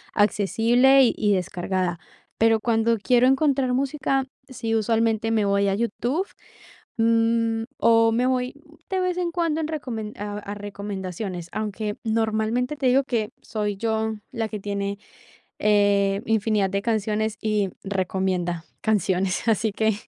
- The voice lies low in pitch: No, high, 220 Hz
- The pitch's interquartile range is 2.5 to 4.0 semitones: Yes, average, 2.8 semitones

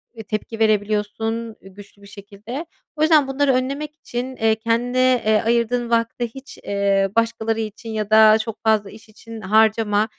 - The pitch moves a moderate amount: No, narrow, 2.2 semitones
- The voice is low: No, high, 225 Hz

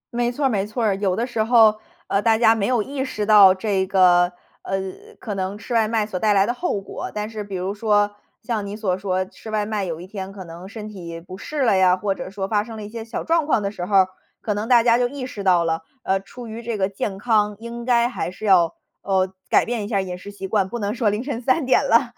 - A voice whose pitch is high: Yes, high, 210 Hz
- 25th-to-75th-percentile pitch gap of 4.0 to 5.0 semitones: No, average, 3.2 semitones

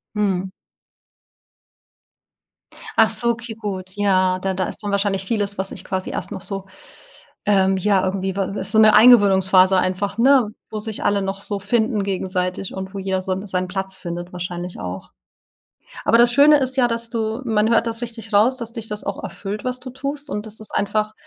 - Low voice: No, high, 205 Hz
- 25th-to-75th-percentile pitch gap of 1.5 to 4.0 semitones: Yes, average, 3.1 semitones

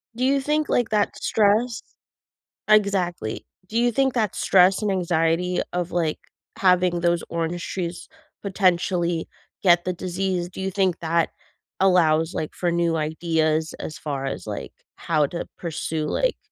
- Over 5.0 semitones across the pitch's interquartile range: No, average, 3.0 semitones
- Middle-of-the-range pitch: Yes, medium, 175 Hz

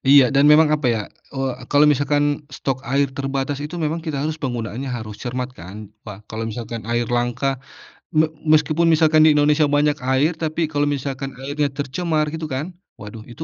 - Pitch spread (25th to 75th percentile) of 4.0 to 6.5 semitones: No, average, 3.3 semitones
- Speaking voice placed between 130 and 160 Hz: Yes, medium, 140 Hz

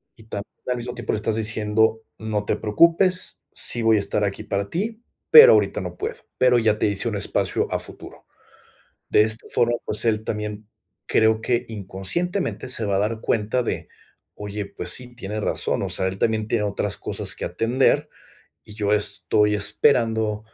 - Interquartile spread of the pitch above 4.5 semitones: No, narrow, 2.5 semitones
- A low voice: Yes, low, 110 Hz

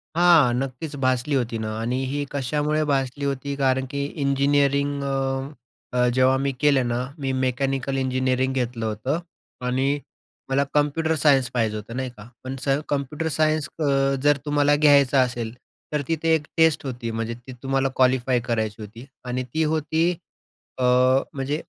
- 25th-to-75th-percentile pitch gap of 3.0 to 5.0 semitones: No, narrow, 2.5 semitones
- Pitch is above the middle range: No, low, 135 Hz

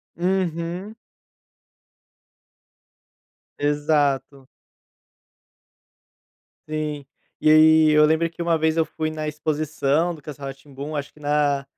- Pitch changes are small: Yes, narrow, 1.7 semitones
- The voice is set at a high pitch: No, medium, 155 Hz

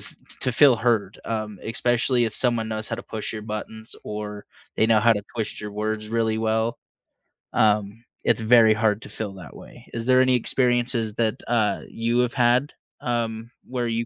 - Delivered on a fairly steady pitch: Yes, narrow, 1.8 semitones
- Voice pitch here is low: Yes, low, 110 Hz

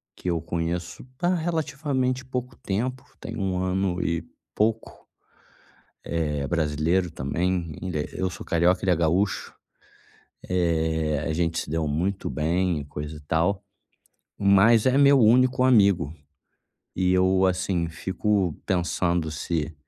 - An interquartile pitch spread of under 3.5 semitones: No, average, 3.8 semitones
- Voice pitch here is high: No, very low, 90 Hz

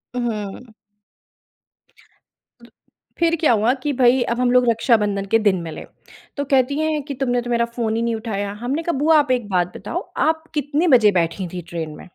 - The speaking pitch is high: Yes, high, 240 Hz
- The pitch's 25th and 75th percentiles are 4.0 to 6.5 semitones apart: Yes, average, 5.2 semitones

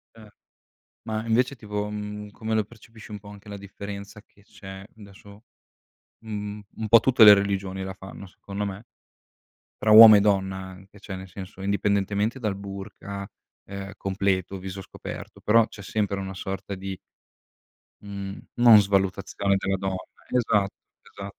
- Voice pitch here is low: Yes, low, 100 Hz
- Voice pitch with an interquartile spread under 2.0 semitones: Yes, narrow, 1.5 semitones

